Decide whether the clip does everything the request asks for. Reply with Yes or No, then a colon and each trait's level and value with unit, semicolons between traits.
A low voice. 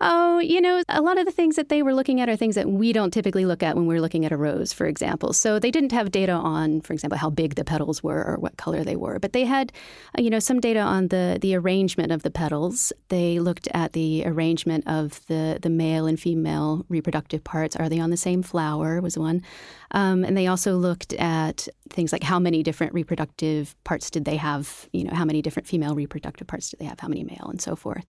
No: medium, 170 Hz